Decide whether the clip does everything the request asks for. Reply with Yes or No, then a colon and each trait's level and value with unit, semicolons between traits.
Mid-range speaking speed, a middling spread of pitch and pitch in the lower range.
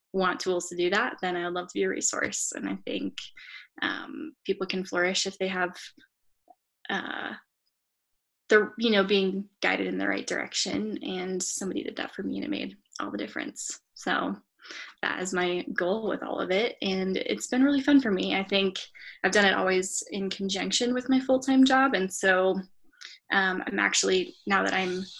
No: average, 195 wpm; average, 3.9 semitones; high, 190 Hz